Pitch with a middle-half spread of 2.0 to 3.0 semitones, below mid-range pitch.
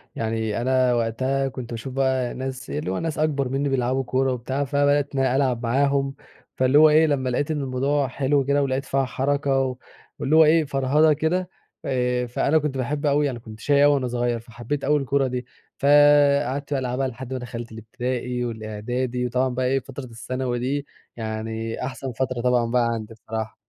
Yes: narrow, 2.5 semitones; low, 130 Hz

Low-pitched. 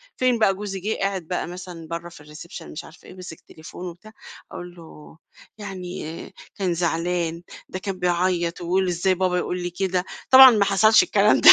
No: medium, 180 Hz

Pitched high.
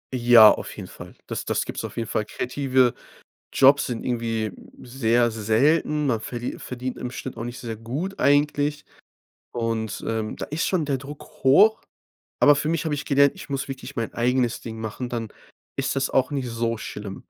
No: low, 125 Hz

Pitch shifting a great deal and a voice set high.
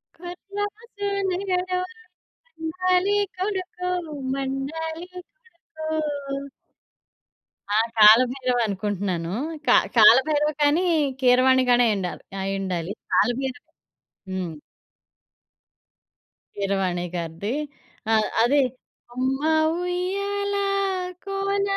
Yes: wide, 8.7 semitones; very high, 290 Hz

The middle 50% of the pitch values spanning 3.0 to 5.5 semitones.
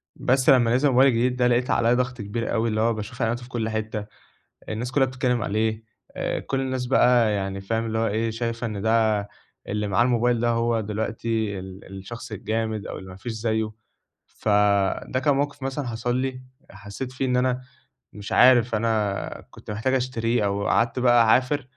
No: narrow, 2.5 semitones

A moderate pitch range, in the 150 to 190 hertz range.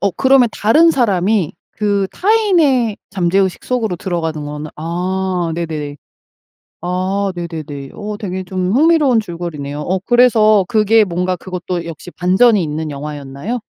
Yes: average, 4.7 semitones; medium, 185 Hz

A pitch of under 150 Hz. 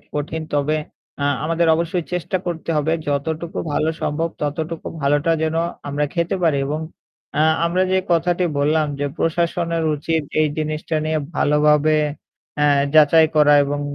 No: medium, 155 Hz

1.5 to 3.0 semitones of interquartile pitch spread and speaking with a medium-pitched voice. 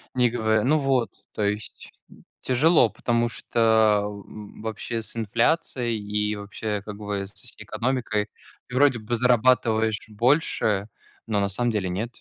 No: narrow, 2.6 semitones; low, 110 Hz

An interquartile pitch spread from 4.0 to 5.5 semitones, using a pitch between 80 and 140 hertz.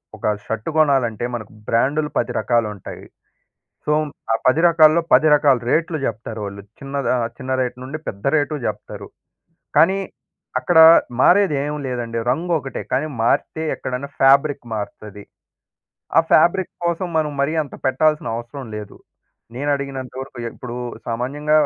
Yes: average, 4.3 semitones; low, 135 Hz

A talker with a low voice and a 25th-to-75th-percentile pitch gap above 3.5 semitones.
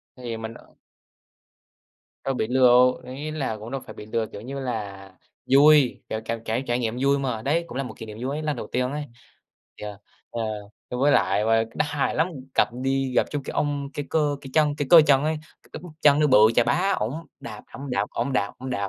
Yes: low, 130 Hz; average, 4.4 semitones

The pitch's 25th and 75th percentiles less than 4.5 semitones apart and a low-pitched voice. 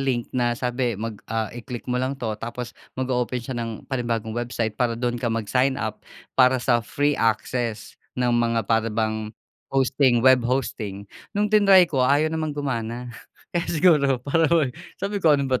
Yes: average, 3.0 semitones; low, 125 Hz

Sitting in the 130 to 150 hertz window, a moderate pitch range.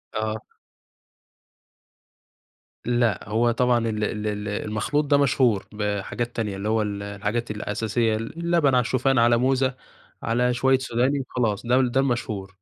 No: low, 115 Hz; average, 3.1 semitones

